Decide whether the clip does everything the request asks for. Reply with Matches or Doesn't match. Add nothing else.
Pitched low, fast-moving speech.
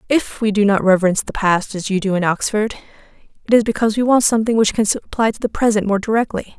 Doesn't match